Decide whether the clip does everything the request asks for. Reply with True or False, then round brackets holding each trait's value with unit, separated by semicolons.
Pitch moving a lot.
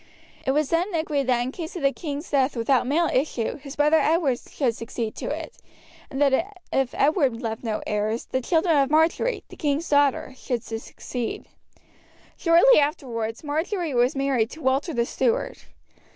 False (4.4 semitones)